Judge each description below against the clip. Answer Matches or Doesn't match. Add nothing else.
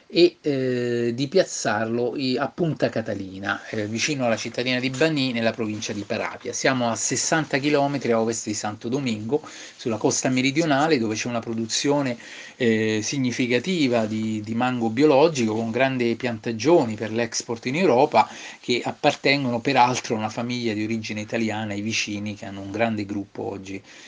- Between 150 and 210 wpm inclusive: Matches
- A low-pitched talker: Matches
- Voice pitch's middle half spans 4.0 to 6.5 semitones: Doesn't match